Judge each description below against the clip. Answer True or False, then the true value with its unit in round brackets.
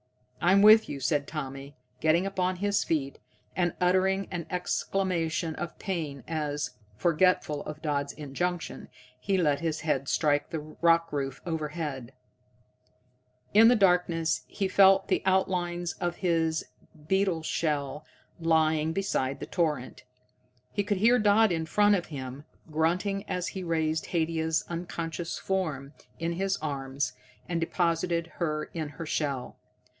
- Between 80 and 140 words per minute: True (135 wpm)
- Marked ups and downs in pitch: False (3.3 semitones)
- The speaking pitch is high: False (165 Hz)